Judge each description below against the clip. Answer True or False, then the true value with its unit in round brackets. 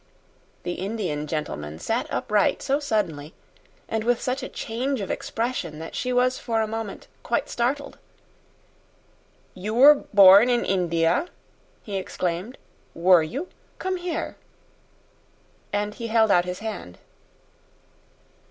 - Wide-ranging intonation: True (5.9 semitones)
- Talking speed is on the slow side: True (125 wpm)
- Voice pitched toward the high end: True (210 Hz)